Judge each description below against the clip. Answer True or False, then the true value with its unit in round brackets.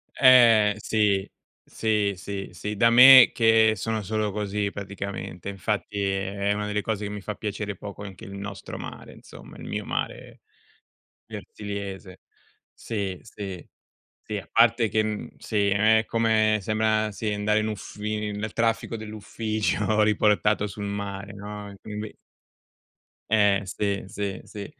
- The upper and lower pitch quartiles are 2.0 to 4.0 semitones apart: False (1.4 semitones)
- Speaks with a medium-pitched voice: False (105 Hz)